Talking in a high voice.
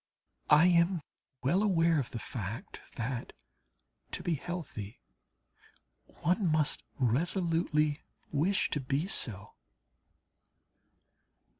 No: medium, 155 Hz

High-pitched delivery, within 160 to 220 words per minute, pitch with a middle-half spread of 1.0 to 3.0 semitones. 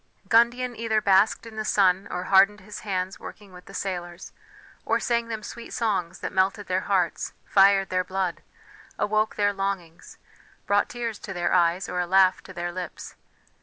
Yes: high, 195 Hz; average, 175 wpm; average, 2.7 semitones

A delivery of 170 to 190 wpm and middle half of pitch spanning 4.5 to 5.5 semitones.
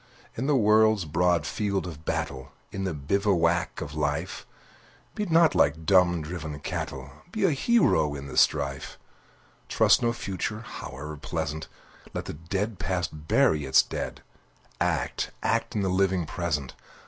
No: average, 150 wpm; average, 5.1 semitones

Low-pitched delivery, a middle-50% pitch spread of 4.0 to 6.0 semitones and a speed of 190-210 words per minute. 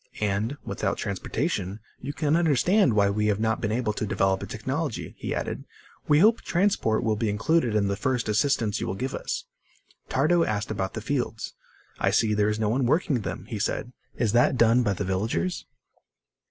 Yes: low, 110 Hz; average, 4.8 semitones; average, 195 wpm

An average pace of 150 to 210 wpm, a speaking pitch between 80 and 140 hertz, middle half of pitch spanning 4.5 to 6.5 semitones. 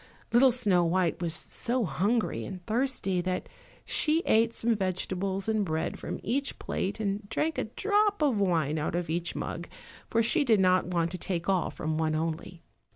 No: average, 180 wpm; high, 190 Hz; average, 5.1 semitones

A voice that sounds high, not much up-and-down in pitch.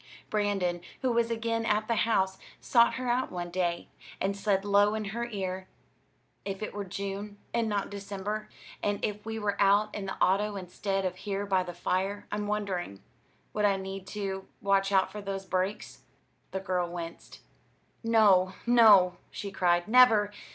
Yes: high, 200 Hz; narrow, 1.9 semitones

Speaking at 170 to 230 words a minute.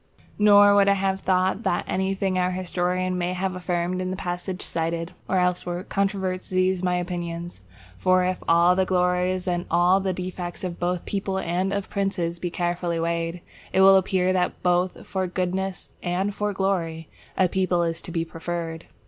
Yes: average, 180 wpm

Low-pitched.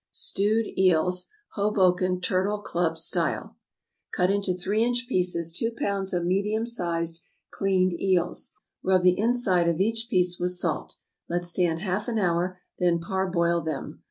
No: medium, 185 Hz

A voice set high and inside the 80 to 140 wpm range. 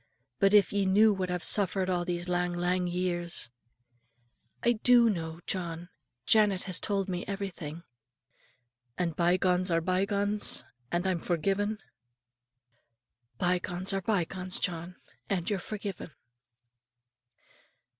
No: medium, 180 Hz; slow, 135 wpm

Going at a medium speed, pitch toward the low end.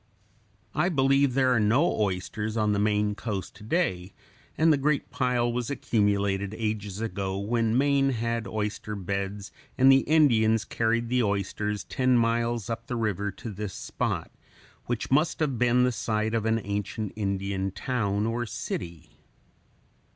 Yes: average, 155 wpm; low, 110 Hz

